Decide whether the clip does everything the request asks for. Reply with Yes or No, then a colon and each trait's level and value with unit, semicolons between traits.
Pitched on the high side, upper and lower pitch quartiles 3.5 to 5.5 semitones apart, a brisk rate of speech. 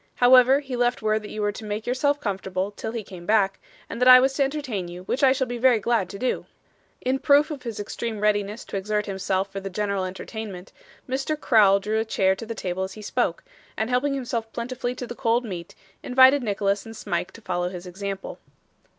Yes: high, 220 Hz; average, 4.3 semitones; fast, 220 wpm